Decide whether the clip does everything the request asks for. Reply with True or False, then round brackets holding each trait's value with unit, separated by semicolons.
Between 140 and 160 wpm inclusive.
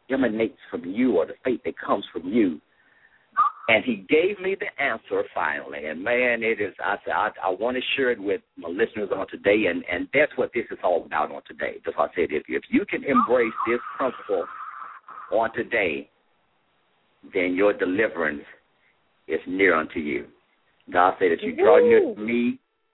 False (185 wpm)